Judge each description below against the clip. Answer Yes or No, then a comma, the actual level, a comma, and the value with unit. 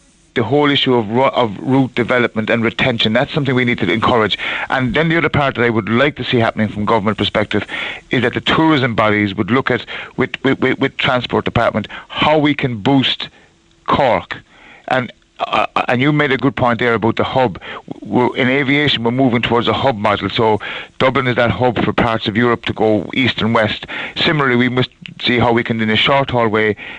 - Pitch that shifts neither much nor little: Yes, average, 3.3 semitones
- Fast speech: Yes, fast, 210 wpm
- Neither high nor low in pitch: No, low, 125 Hz